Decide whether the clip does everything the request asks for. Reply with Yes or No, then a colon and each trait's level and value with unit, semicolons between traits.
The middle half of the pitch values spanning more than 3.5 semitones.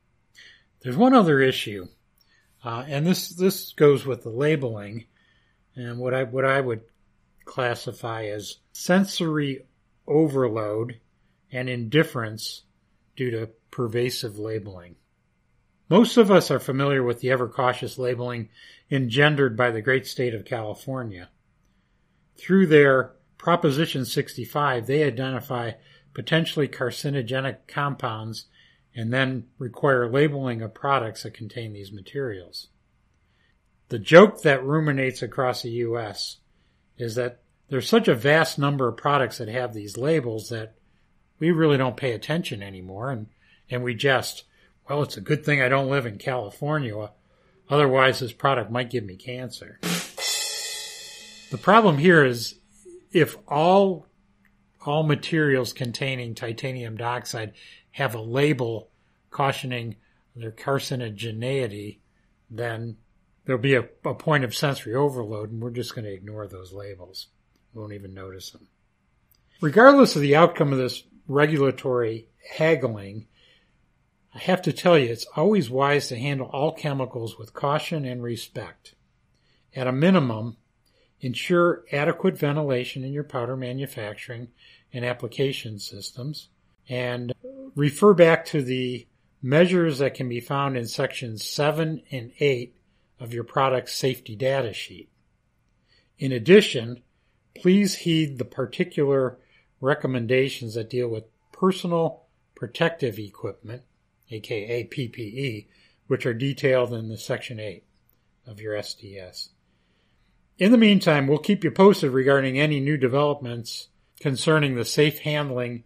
Yes: average, 3.9 semitones